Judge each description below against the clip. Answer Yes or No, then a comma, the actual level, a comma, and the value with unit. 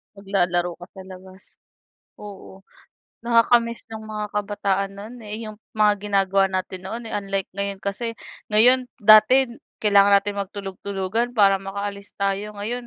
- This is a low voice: No, high, 200 Hz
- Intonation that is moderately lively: No, narrow, 1.7 semitones